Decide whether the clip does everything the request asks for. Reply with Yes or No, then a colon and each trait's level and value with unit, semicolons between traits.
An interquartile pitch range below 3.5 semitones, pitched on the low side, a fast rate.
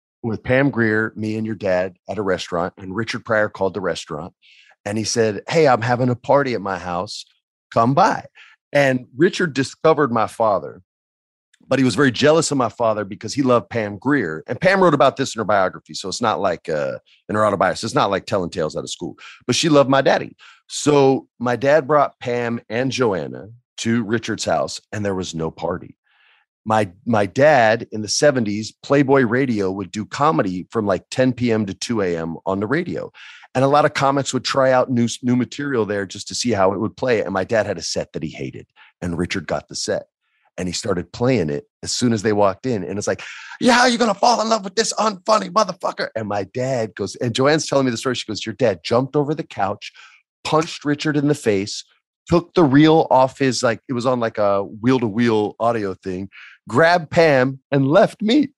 No: average, 5.2 semitones; low, 120 Hz; fast, 220 wpm